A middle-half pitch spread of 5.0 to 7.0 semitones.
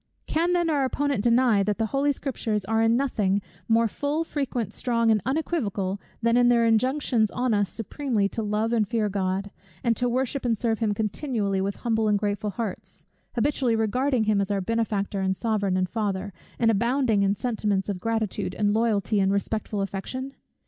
No: average, 3.4 semitones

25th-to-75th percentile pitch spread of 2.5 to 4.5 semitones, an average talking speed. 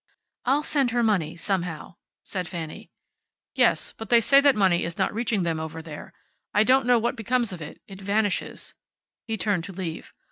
No: wide, 5.5 semitones; average, 185 wpm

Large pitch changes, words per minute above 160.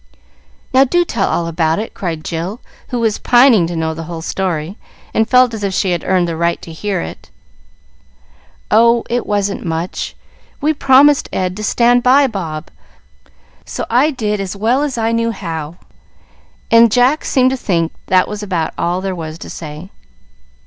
Yes: wide, 6.1 semitones; average, 175 wpm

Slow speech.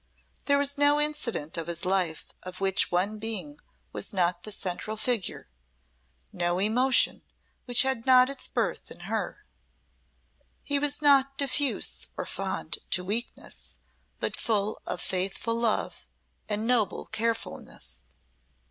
Yes: slow, 130 wpm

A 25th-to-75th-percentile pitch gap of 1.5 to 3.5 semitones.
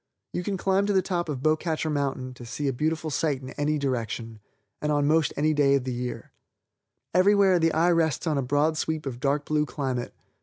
Yes: average, 3.1 semitones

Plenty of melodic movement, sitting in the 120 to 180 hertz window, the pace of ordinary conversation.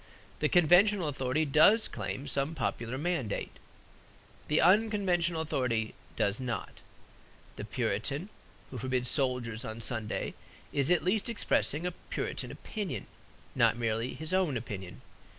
No: wide, 7.0 semitones; medium, 140 Hz; slow, 120 wpm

